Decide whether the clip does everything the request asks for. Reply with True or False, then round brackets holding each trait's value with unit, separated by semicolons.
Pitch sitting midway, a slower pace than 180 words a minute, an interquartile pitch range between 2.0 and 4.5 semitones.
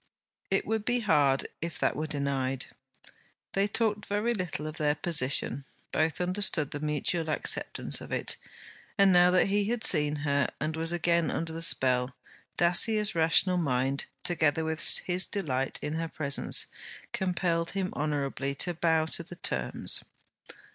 True (160 Hz; 155 wpm; 3.8 semitones)